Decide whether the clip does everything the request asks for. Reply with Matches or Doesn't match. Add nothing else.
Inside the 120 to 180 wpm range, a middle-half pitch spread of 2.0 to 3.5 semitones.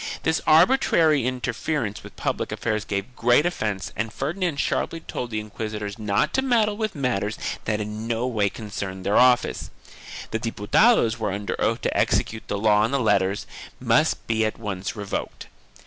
Doesn't match